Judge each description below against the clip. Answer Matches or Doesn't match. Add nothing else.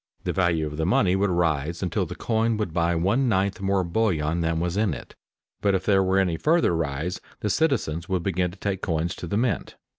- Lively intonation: Doesn't match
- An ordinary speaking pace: Doesn't match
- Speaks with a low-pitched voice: Matches